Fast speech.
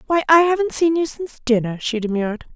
Yes: fast, 210 wpm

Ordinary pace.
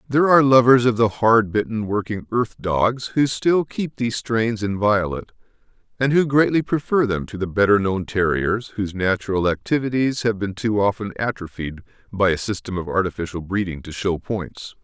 Yes: average, 175 wpm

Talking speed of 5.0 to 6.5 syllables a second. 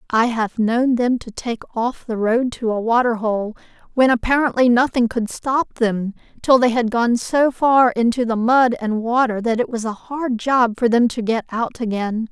No: 4.4 syllables/s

